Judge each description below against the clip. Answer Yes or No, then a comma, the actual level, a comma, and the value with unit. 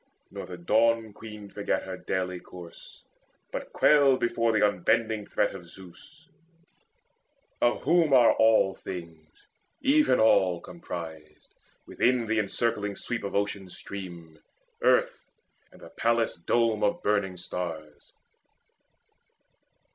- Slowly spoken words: Yes, slow, 115 wpm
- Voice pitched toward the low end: Yes, low, 105 Hz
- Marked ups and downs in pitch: No, average, 4.3 semitones